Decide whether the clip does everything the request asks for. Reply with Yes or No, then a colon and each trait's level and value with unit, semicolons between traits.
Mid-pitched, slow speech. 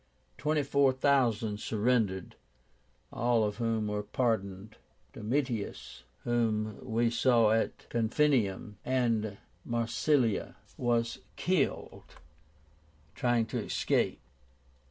No: low, 115 Hz; slow, 90 wpm